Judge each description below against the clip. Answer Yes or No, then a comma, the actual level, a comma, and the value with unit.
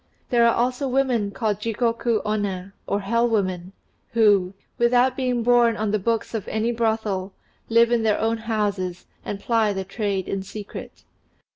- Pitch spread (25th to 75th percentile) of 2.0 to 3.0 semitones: Yes, average, 2.7 semitones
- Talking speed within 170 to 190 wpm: No, average, 160 wpm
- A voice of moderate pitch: No, high, 220 Hz